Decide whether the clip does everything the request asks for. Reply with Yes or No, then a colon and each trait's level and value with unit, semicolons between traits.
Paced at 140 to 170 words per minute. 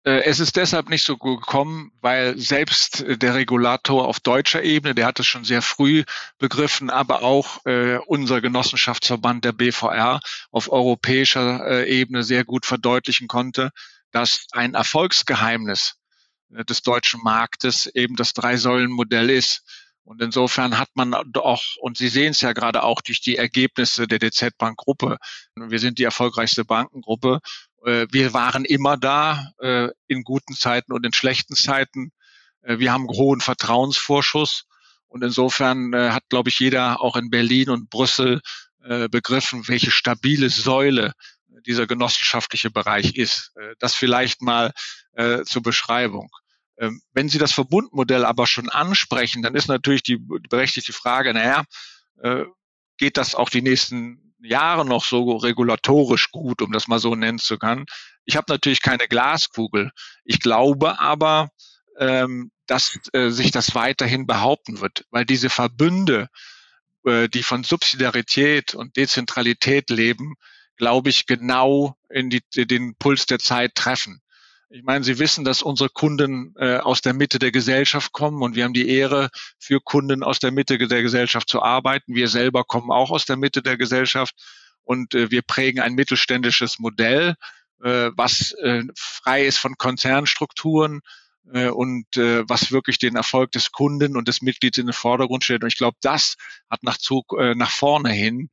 Yes: average, 150 wpm